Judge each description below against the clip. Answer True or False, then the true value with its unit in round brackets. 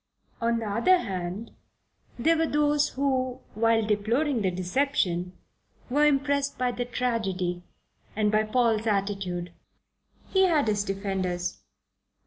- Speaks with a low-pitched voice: False (225 Hz)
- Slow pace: True (120 wpm)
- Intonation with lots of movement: True (5.9 semitones)